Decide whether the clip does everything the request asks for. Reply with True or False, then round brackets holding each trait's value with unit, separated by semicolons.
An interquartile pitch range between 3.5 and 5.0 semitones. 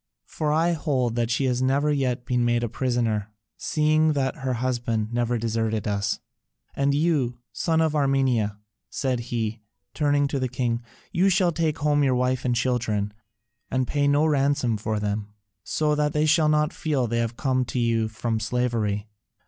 True (4.1 semitones)